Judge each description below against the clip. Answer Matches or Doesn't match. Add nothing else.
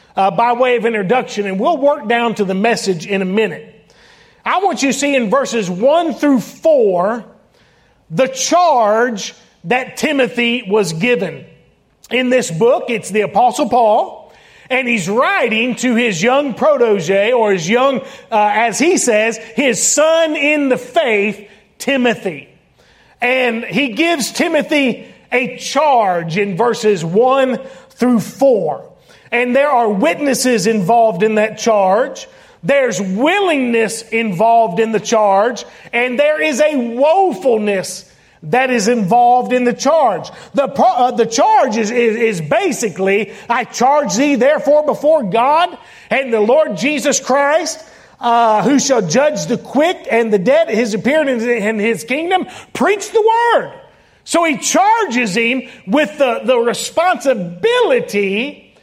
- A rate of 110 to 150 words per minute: Matches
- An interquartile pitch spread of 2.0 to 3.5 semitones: Doesn't match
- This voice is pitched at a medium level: Doesn't match